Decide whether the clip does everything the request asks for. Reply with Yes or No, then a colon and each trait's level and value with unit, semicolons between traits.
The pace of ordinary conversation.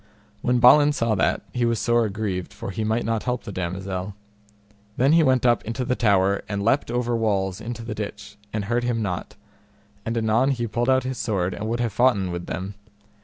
No: fast, 210 wpm